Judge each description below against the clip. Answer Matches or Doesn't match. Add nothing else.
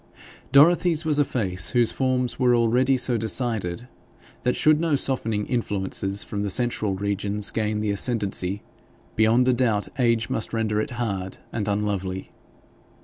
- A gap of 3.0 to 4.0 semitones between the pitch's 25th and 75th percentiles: Matches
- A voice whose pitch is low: Matches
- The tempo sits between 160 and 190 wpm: Doesn't match